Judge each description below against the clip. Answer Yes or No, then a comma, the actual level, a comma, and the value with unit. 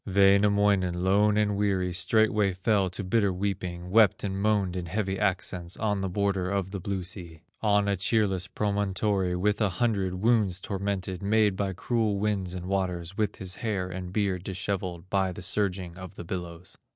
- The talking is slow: No, average, 175 wpm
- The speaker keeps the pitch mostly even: Yes, narrow, 2.0 semitones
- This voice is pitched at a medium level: No, very low, 95 Hz